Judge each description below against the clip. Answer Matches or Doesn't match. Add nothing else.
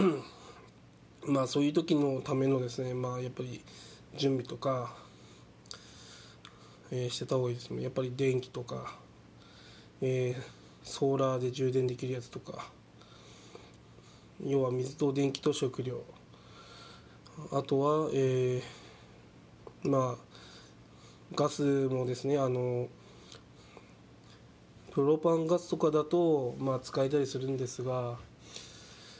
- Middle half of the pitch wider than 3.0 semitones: Doesn't match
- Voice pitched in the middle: Doesn't match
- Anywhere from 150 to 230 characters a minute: Matches